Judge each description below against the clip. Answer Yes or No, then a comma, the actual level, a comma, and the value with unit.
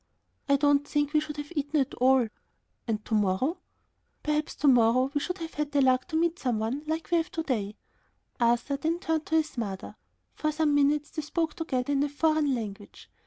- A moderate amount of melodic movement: Yes, average, 3.6 semitones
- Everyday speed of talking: No, fast, 210 wpm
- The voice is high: Yes, very high, 290 Hz